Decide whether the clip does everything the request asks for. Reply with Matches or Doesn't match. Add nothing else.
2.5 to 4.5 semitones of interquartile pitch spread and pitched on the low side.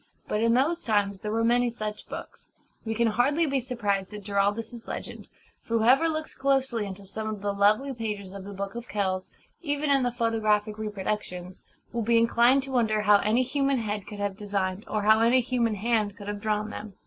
Doesn't match